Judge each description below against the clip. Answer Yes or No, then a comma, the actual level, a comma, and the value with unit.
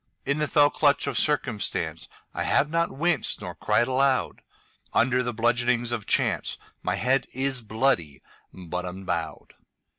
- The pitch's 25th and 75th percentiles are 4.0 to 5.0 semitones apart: Yes, average, 4.6 semitones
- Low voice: Yes, low, 125 Hz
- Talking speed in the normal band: No, slow, 125 wpm